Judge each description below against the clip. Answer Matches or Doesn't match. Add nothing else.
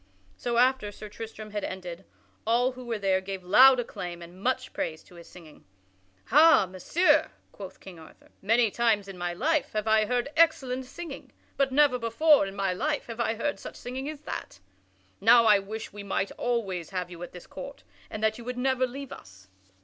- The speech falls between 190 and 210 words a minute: Matches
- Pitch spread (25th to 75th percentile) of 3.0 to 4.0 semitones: Doesn't match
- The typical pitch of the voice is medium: Doesn't match